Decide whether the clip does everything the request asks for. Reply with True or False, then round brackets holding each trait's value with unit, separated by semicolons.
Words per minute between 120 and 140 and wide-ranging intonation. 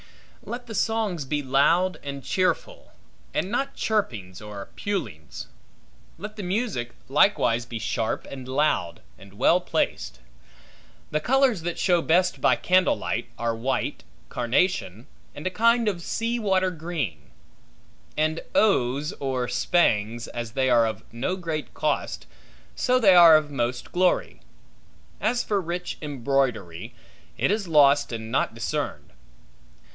True (135 wpm; 7.6 semitones)